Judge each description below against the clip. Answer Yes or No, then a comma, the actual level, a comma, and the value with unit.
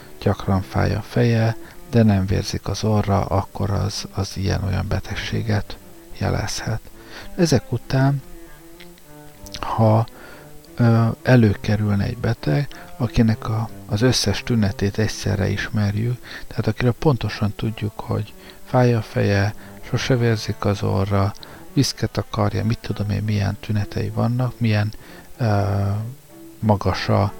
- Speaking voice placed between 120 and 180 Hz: No, low, 110 Hz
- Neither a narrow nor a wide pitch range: Yes, average, 3.1 semitones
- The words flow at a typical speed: Yes, average, 115 wpm